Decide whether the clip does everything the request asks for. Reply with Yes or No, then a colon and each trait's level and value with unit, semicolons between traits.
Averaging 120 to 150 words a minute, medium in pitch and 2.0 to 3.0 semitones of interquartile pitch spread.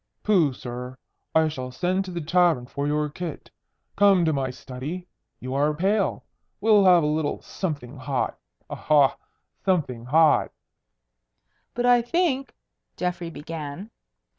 No: average, 140 wpm; medium, 160 Hz; average, 4.8 semitones